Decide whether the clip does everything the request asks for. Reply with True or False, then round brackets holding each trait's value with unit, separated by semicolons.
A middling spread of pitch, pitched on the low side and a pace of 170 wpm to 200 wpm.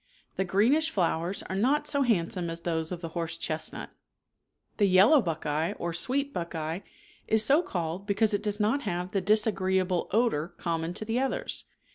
False (4.6 semitones; 190 Hz; 175 wpm)